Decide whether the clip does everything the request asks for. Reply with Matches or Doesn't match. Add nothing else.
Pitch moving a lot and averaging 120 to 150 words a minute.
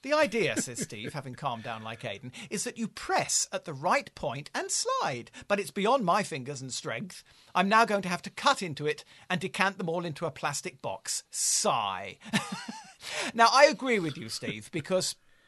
Doesn't match